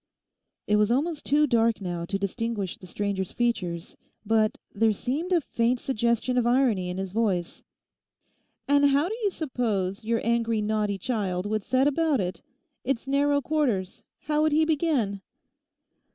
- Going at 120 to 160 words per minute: Yes, average, 155 wpm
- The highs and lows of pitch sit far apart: Yes, wide, 5.7 semitones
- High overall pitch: Yes, high, 230 Hz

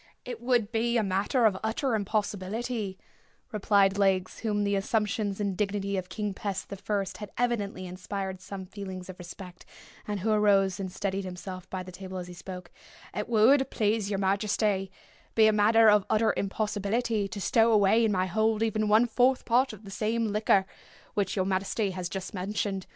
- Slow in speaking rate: No, average, 180 wpm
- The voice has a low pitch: No, high, 205 Hz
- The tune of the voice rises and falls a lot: No, narrow, 2.4 semitones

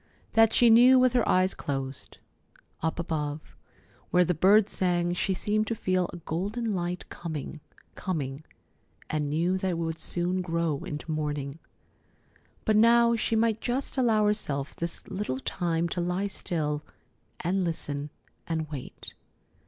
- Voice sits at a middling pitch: Yes, medium, 175 Hz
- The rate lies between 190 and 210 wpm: No, average, 145 wpm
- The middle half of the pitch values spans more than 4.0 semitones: Yes, average, 5.1 semitones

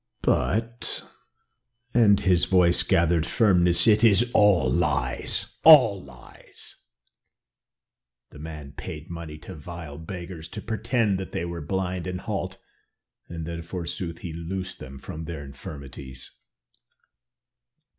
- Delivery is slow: Yes, slow, 120 wpm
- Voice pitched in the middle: No, very low, 85 Hz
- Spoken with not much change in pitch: No, average, 3.6 semitones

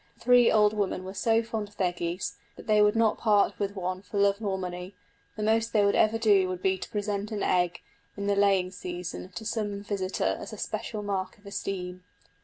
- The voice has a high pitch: Yes, high, 200 Hz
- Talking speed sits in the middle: No, fast, 220 wpm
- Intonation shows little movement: Yes, narrow, 2.3 semitones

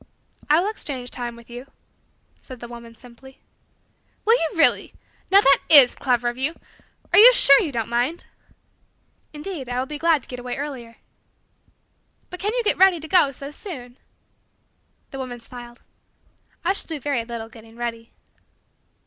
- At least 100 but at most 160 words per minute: No, average, 170 wpm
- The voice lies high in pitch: Yes, very high, 265 Hz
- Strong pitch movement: No, average, 5.0 semitones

